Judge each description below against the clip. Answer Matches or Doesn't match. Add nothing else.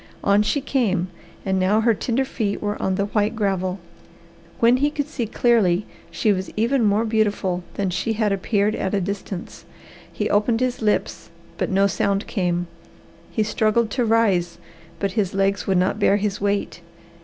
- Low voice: Doesn't match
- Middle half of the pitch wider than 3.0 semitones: Doesn't match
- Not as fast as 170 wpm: Doesn't match